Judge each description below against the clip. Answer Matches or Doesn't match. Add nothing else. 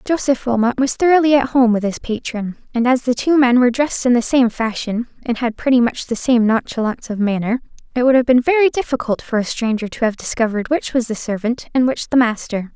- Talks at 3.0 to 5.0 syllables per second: Doesn't match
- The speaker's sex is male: Doesn't match